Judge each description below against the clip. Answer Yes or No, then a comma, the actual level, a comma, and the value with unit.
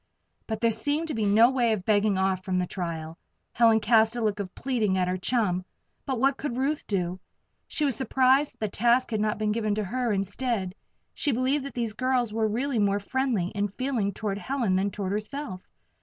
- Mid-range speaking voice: No, high, 220 Hz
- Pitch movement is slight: No, average, 4.3 semitones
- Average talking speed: No, fast, 210 wpm